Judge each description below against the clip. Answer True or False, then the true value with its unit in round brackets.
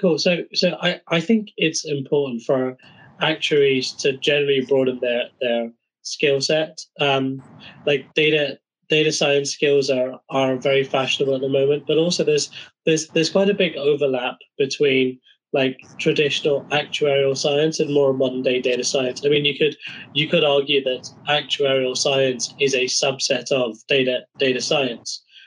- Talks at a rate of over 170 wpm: False (155 wpm)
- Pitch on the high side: False (140 Hz)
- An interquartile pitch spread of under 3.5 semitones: True (2.7 semitones)